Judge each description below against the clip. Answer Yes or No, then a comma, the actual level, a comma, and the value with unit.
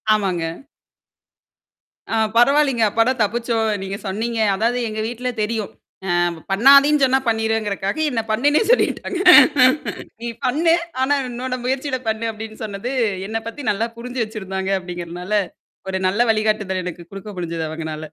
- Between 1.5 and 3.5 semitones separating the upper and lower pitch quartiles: No, average, 4.2 semitones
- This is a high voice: Yes, high, 220 Hz